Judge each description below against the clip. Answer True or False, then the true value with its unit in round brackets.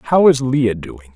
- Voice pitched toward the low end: True (120 Hz)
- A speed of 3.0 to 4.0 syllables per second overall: True (3.6 syllables/s)